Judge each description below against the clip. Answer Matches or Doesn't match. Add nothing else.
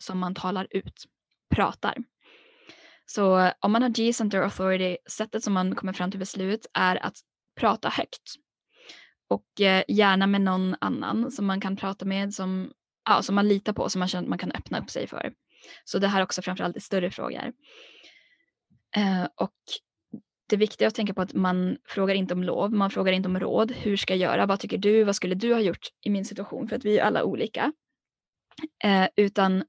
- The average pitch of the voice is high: Matches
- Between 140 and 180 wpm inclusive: Doesn't match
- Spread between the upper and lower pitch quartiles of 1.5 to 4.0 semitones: Matches